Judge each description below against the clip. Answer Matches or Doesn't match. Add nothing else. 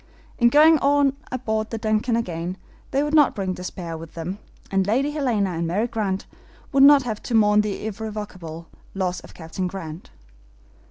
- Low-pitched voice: Doesn't match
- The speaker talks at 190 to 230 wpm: Doesn't match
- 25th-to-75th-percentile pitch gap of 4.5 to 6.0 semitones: Matches